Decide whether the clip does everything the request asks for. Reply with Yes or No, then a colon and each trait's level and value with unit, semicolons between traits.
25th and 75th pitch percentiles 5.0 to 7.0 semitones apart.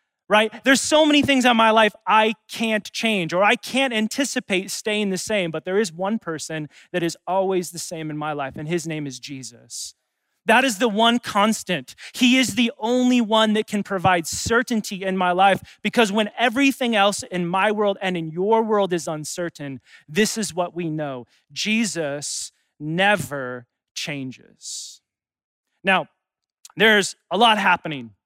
Yes: wide, 5.5 semitones